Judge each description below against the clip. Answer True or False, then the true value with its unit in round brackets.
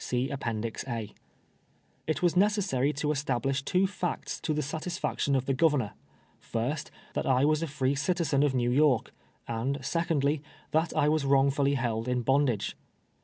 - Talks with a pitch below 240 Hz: True (140 Hz)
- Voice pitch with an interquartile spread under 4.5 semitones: True (3.4 semitones)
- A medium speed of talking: True (165 wpm)